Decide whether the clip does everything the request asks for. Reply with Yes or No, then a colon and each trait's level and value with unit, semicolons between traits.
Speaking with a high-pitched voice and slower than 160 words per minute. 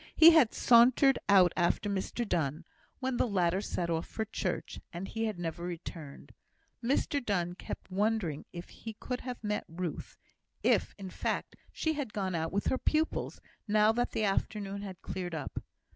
No: high, 200 Hz; average, 175 wpm